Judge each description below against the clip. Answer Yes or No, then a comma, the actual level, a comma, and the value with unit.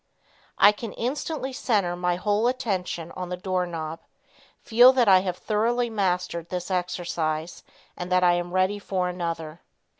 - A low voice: No, medium, 185 Hz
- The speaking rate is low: No, average, 155 wpm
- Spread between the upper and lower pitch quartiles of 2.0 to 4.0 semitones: Yes, average, 3.2 semitones